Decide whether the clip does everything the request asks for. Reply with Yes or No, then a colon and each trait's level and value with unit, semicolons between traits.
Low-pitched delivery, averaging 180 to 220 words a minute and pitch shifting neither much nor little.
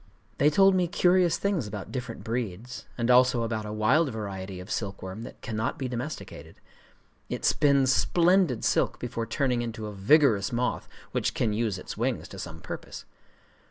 No: low, 120 Hz; average, 160 wpm; average, 4.7 semitones